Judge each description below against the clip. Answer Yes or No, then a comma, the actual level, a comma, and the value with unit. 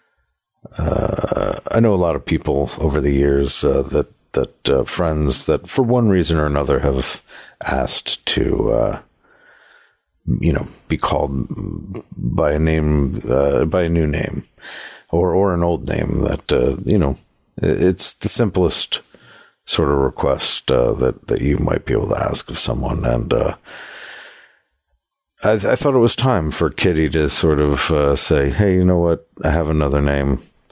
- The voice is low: Yes, very low, 80 Hz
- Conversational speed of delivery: Yes, average, 170 wpm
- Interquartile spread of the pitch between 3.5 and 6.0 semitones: Yes, average, 3.9 semitones